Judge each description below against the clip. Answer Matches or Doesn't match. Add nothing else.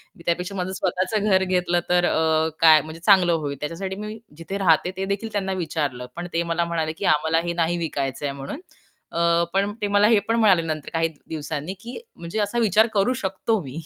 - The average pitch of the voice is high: Doesn't match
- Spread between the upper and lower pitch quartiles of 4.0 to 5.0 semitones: Doesn't match